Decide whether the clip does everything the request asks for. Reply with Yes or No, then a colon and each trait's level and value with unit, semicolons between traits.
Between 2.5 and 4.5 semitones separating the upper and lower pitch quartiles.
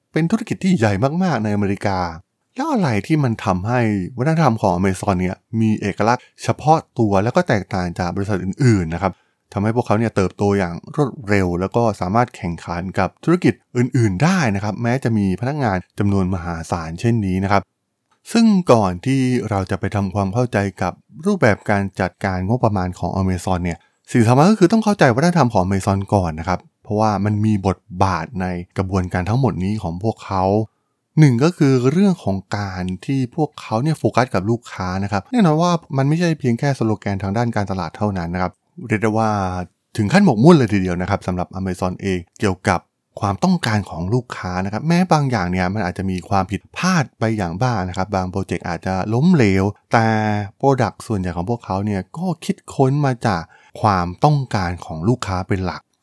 No: average, 5.1 semitones